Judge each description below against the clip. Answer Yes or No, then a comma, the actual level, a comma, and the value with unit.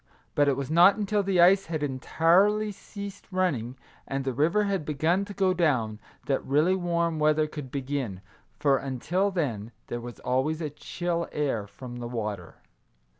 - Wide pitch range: Yes, wide, 5.9 semitones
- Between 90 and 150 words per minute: No, average, 170 wpm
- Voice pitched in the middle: Yes, medium, 155 Hz